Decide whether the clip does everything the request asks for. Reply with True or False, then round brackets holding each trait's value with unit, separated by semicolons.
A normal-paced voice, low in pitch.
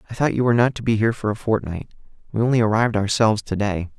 False (255 wpm; 110 Hz)